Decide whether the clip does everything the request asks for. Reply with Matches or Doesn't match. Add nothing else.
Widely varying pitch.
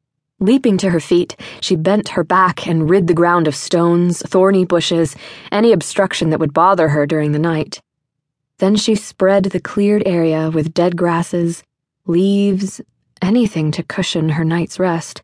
Doesn't match